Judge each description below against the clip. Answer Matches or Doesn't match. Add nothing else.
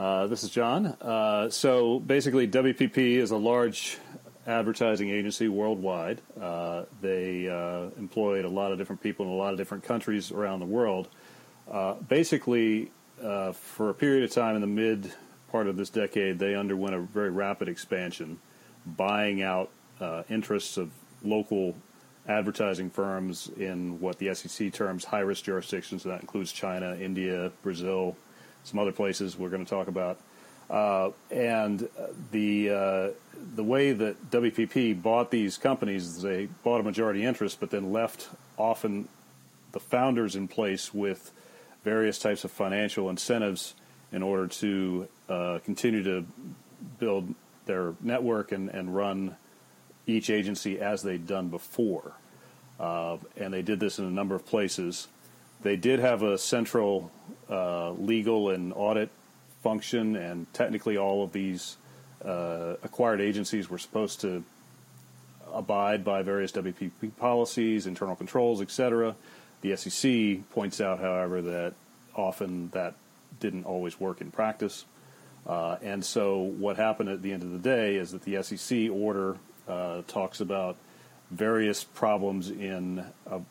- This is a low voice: Matches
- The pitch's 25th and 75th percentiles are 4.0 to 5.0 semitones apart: Doesn't match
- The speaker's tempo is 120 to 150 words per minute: Matches